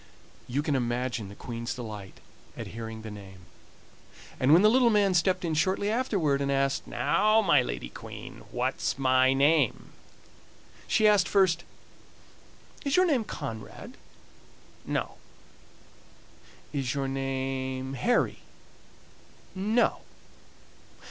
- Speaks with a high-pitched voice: No, low, 135 Hz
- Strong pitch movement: Yes, wide, 8.2 semitones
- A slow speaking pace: Yes, slow, 115 wpm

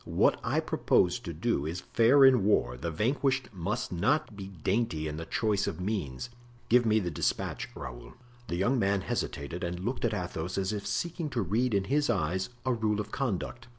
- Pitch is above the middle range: No, low, 100 Hz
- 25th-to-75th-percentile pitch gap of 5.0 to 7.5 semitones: Yes, wide, 5.6 semitones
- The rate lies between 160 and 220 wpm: Yes, average, 195 wpm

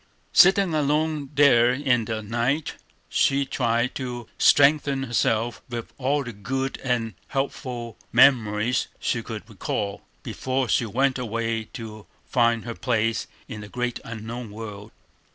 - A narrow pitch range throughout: No, average, 3.0 semitones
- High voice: No, low, 120 Hz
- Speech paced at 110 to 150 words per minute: Yes, slow, 135 wpm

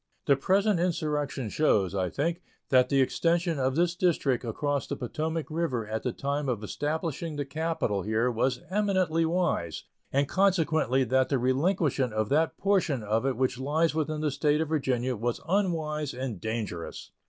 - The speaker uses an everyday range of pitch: Yes, average, 4.6 semitones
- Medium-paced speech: Yes, average, 165 wpm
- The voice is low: No, medium, 145 Hz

